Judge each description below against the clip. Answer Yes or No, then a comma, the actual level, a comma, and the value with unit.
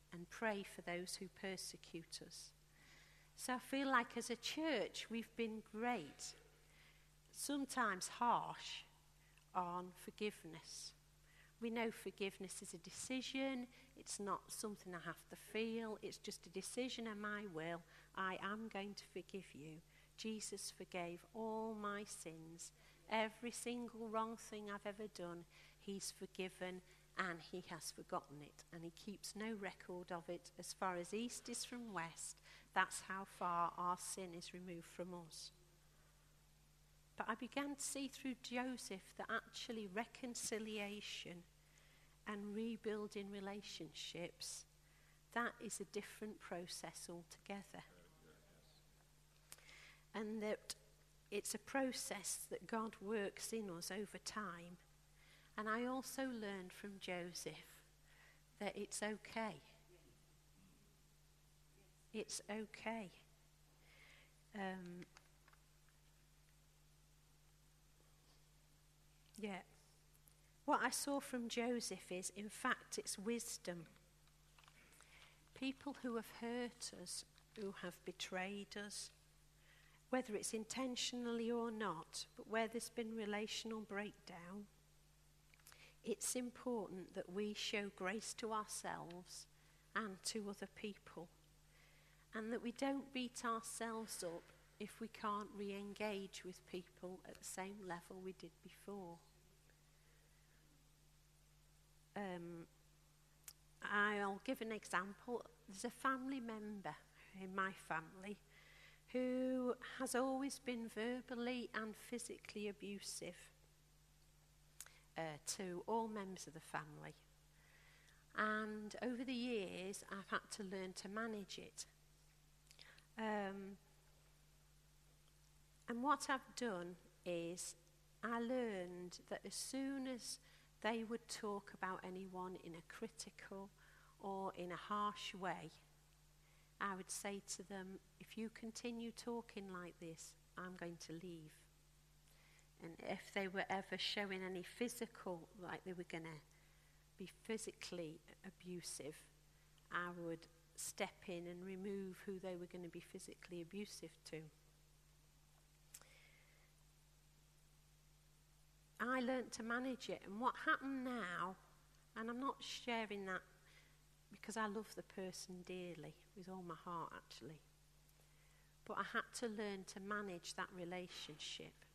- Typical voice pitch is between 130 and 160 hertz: No, high, 190 Hz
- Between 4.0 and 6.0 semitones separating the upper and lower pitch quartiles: Yes, average, 5.0 semitones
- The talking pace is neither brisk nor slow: No, slow, 120 wpm